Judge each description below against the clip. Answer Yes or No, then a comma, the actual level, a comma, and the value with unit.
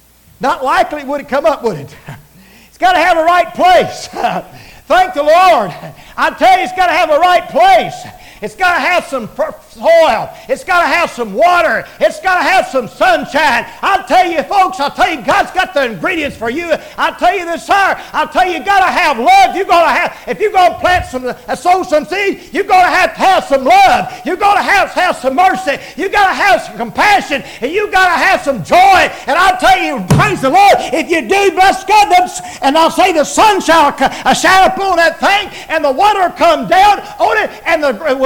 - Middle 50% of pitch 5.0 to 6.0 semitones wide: No, average, 4.0 semitones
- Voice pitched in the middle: No, very high, 345 Hz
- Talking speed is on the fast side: Yes, fast, 225 wpm